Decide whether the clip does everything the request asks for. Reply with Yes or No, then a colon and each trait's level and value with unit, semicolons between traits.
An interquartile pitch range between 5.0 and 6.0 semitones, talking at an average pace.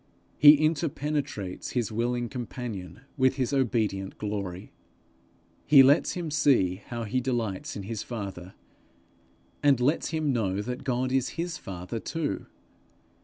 No: wide, 5.5 semitones; slow, 130 wpm